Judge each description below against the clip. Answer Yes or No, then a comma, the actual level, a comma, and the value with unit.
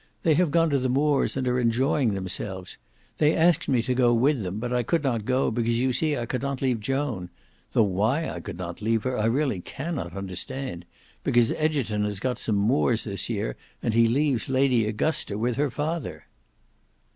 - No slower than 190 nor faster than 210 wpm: Yes, average, 200 wpm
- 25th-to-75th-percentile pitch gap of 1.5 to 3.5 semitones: No, average, 4.4 semitones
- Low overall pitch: Yes, low, 125 Hz